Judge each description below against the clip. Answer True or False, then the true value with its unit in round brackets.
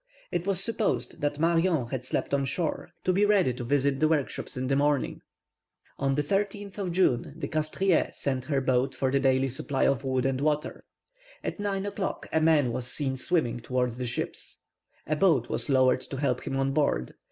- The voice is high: False (140 Hz)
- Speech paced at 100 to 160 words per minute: False (195 wpm)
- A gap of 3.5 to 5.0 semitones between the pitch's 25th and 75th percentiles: True (4.3 semitones)